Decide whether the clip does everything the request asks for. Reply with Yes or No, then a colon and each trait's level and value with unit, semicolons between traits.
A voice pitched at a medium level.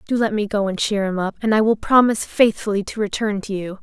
No: high, 210 Hz